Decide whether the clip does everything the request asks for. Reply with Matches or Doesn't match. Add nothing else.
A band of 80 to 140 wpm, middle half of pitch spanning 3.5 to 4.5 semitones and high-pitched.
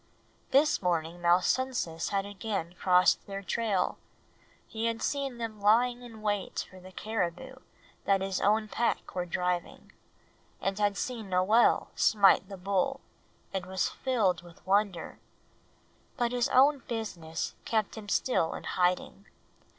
Matches